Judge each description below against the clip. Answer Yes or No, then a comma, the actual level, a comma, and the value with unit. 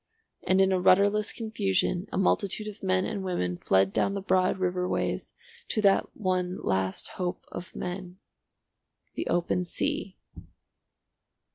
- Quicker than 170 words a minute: No, slow, 135 wpm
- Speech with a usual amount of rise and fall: No, narrow, 1.6 semitones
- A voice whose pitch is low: No, medium, 185 Hz